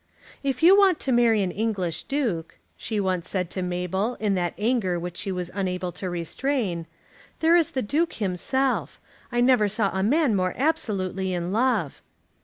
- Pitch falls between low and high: No, high, 205 Hz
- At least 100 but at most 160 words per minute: No, average, 175 wpm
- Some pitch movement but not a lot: No, wide, 5.8 semitones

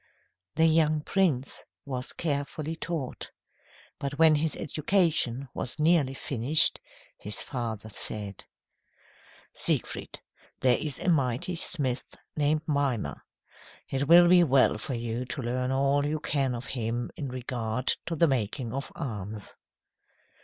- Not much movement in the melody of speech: No, average, 4.1 semitones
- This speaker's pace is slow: Yes, slow, 130 wpm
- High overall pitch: No, low, 135 Hz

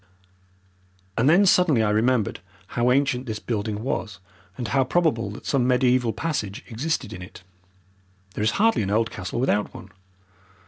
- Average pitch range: Yes, average, 4.1 semitones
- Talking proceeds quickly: No, average, 155 wpm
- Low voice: Yes, low, 120 Hz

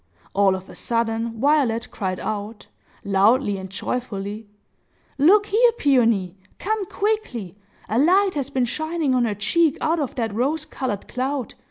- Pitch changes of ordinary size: No, wide, 6.9 semitones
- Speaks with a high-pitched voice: Yes, high, 245 Hz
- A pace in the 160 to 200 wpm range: No, average, 145 wpm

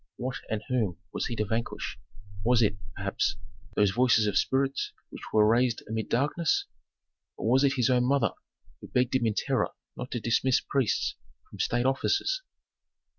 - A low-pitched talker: Yes, low, 125 Hz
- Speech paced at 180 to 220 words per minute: No, average, 170 wpm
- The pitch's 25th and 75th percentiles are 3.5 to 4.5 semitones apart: No, average, 2.9 semitones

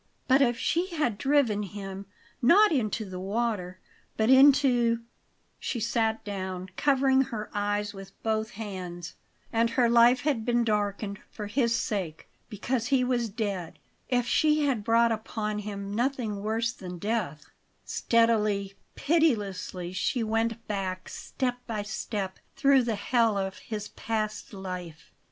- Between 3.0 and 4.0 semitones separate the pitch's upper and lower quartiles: Yes, average, 3.3 semitones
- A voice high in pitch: Yes, high, 220 Hz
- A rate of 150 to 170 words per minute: No, average, 140 wpm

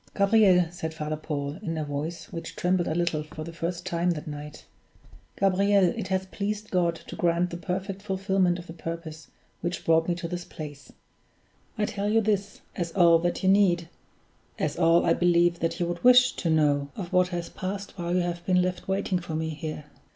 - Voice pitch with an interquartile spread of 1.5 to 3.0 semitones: Yes, narrow, 2.5 semitones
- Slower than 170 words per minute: No, average, 200 wpm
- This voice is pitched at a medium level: Yes, medium, 175 Hz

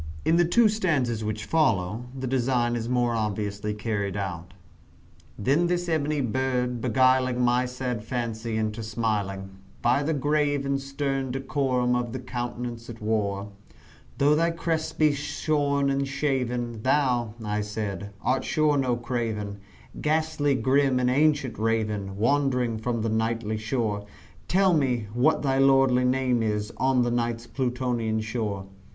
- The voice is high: No, low, 125 Hz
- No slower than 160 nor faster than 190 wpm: No, average, 145 wpm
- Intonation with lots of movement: No, average, 3.8 semitones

